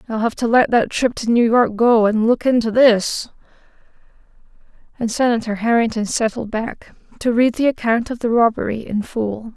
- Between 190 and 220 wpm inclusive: No, average, 175 wpm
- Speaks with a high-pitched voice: Yes, high, 230 Hz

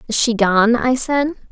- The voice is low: No, high, 240 Hz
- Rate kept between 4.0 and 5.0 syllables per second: Yes, 4.4 syllables/s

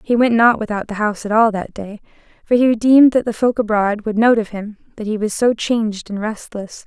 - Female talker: Yes, female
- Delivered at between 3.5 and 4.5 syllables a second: No, 5.6 syllables/s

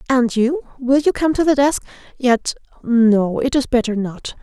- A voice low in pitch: No, very high, 255 Hz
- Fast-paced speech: No, average, 165 wpm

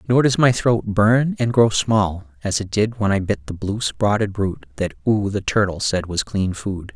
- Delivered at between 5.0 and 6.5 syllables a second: No, 4.4 syllables/s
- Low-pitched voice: Yes, low, 105 Hz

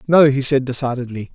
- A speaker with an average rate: Yes, average, 180 wpm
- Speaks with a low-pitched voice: Yes, low, 130 Hz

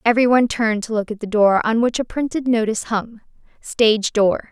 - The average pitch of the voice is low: No, high, 225 Hz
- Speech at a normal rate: No, fast, 210 wpm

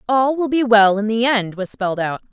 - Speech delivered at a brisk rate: Yes, fast, 260 wpm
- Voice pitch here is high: Yes, high, 225 Hz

